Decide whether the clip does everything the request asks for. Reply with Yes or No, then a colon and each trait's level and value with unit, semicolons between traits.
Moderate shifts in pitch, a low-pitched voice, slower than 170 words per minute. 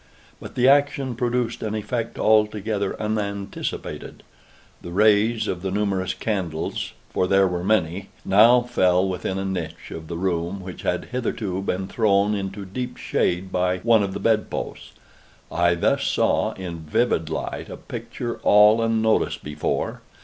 Yes: average, 3.2 semitones; low, 100 Hz; average, 150 wpm